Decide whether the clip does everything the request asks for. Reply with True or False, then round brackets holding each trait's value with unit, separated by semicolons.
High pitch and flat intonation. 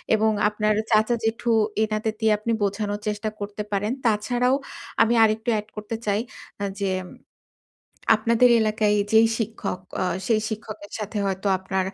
True (215 Hz; 1.3 semitones)